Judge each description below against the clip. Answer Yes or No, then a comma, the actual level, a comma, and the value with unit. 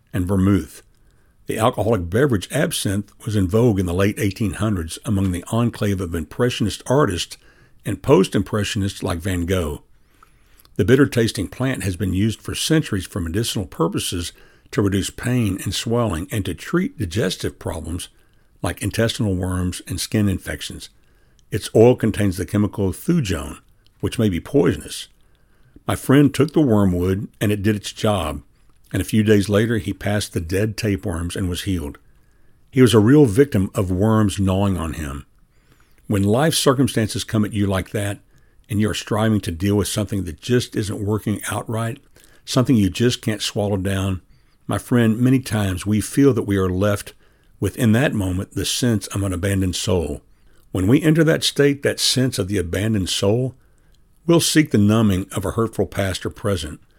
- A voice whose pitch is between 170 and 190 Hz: No, low, 105 Hz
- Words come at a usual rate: Yes, average, 170 wpm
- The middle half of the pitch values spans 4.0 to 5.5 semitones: No, average, 3.2 semitones